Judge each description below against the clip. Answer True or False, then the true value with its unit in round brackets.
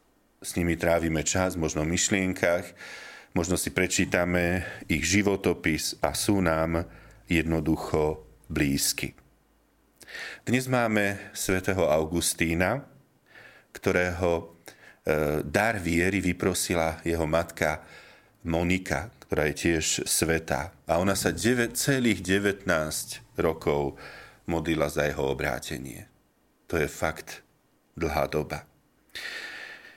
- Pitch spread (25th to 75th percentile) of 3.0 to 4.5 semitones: True (3.5 semitones)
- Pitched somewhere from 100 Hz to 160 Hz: False (85 Hz)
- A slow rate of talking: True (95 wpm)